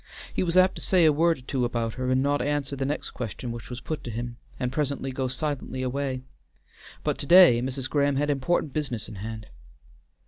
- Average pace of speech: No, fast, 215 wpm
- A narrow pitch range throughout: No, average, 3.0 semitones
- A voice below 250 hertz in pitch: Yes, low, 135 Hz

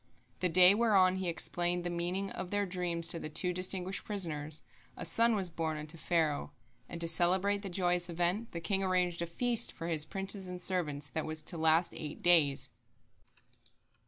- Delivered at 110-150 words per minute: No, average, 185 wpm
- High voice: No, medium, 175 Hz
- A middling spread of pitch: No, narrow, 2.3 semitones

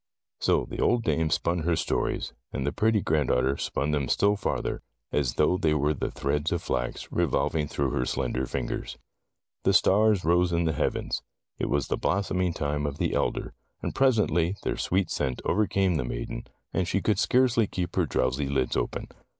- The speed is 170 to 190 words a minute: Yes, average, 185 wpm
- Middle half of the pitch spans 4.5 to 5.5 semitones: Yes, average, 5.2 semitones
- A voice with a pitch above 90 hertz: No, very low, 80 Hz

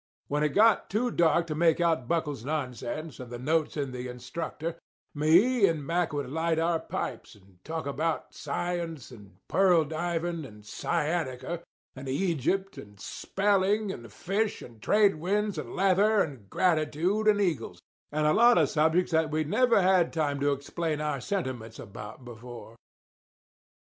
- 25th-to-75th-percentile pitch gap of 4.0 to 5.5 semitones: Yes, average, 5.0 semitones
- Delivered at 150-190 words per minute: Yes, average, 160 wpm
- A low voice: No, medium, 160 Hz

